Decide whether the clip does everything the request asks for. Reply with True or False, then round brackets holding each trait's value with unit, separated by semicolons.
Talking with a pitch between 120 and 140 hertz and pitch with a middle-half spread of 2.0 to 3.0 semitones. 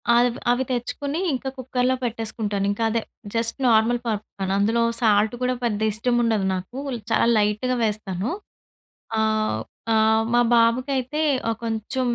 False (225 Hz; 2.5 semitones)